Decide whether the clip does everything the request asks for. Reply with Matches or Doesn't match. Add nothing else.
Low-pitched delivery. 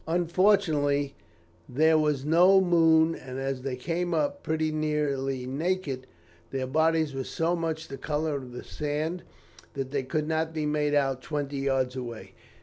Doesn't match